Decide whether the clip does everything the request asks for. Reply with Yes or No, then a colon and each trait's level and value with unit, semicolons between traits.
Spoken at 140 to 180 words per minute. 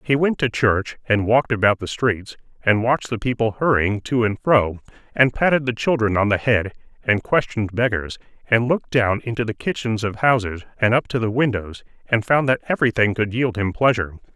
No: average, 200 wpm